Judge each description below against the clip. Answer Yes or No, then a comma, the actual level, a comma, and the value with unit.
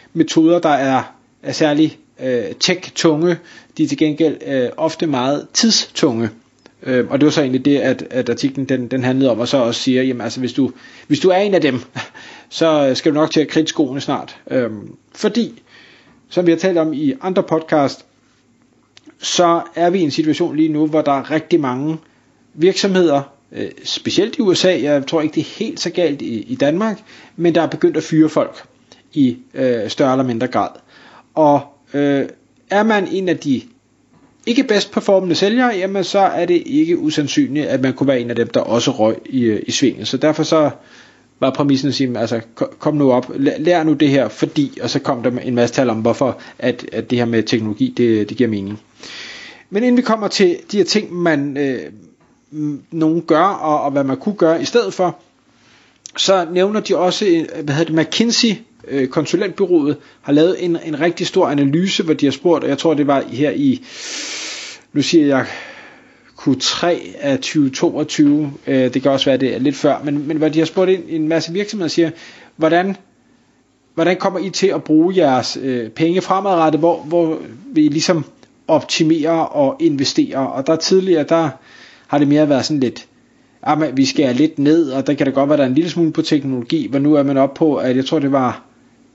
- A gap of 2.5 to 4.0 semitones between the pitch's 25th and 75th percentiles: No, average, 5.0 semitones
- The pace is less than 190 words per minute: No, average, 205 wpm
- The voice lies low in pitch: No, medium, 160 Hz